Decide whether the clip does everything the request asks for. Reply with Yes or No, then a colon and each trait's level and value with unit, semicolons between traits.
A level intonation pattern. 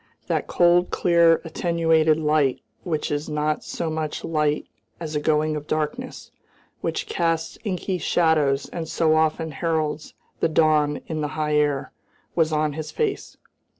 Yes: narrow, 1.6 semitones